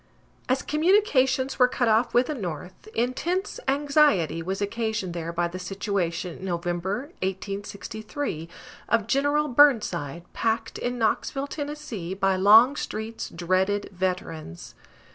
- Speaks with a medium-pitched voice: No, high, 215 Hz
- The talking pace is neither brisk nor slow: No, slow, 120 wpm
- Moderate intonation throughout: No, wide, 6.3 semitones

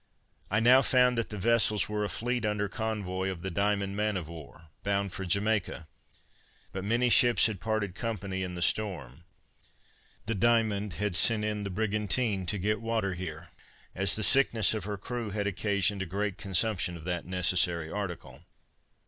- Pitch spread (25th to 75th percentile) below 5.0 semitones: Yes, average, 2.7 semitones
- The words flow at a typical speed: Yes, average, 175 wpm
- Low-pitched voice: Yes, low, 100 Hz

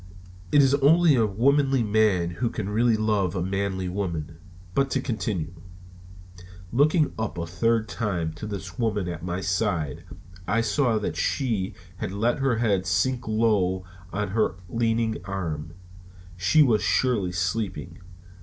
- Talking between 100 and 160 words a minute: Yes, average, 145 wpm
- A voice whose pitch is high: No, low, 105 Hz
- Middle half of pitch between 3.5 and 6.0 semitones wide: Yes, average, 4.1 semitones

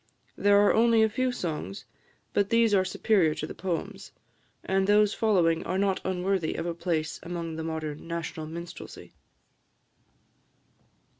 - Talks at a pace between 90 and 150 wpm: Yes, average, 145 wpm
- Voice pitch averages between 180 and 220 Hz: Yes, medium, 185 Hz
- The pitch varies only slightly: No, average, 3.7 semitones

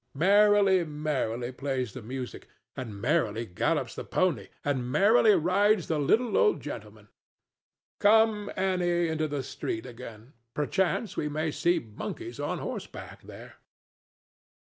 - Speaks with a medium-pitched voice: Yes, medium, 155 Hz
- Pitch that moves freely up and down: Yes, wide, 7.5 semitones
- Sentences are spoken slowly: Yes, slow, 125 wpm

